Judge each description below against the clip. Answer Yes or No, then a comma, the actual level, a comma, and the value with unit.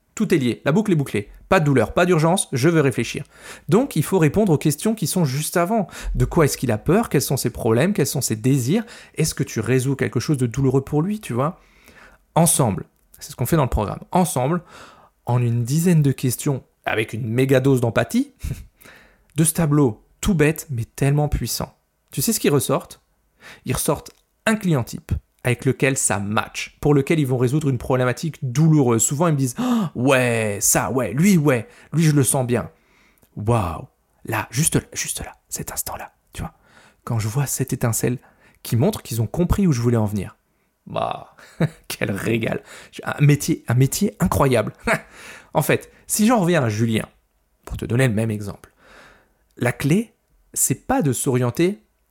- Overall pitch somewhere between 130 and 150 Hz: Yes, medium, 140 Hz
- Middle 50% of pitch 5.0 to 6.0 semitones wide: Yes, average, 5.3 semitones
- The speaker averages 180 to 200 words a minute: Yes, average, 195 wpm